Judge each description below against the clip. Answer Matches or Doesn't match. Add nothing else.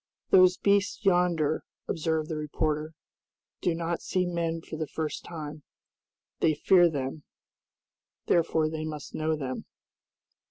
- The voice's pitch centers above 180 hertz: Doesn't match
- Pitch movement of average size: Doesn't match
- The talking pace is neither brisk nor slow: Doesn't match